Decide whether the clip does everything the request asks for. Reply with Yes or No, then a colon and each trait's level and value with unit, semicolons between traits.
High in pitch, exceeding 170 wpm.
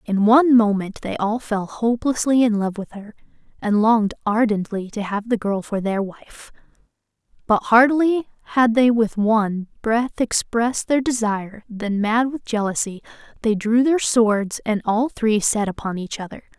No: high, 220 Hz; average, 165 wpm